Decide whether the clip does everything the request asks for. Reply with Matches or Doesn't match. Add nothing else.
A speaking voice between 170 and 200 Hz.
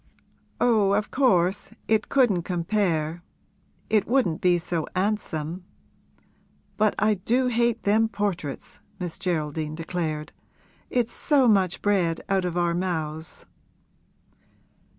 Matches